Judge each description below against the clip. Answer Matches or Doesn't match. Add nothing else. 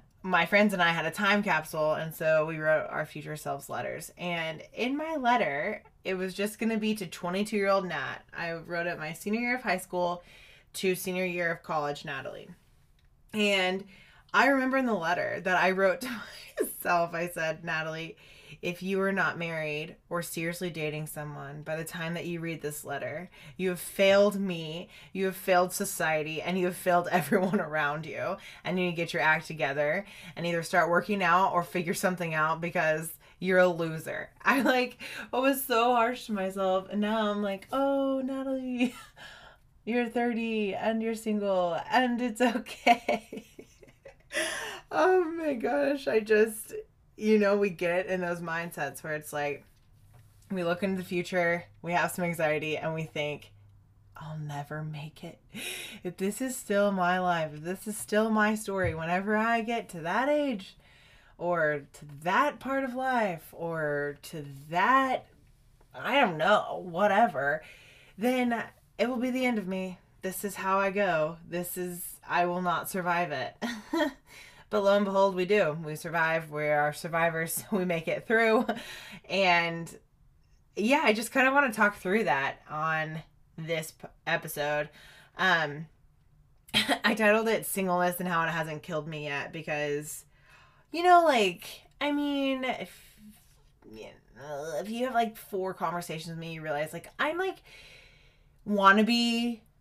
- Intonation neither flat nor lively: Matches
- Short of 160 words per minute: Doesn't match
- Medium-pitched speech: Matches